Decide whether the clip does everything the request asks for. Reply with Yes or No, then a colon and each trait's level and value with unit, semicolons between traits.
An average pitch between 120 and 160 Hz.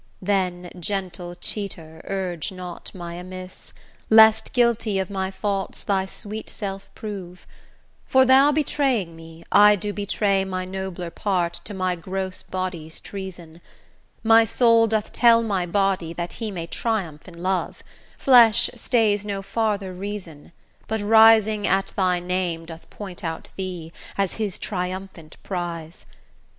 No: high, 190 Hz